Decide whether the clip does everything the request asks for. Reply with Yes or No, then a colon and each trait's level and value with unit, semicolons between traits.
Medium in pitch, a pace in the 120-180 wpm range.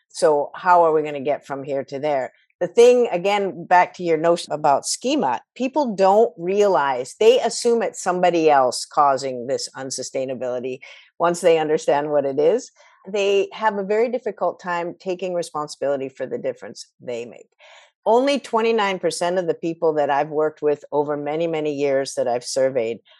Yes: medium, 170 Hz; average, 170 wpm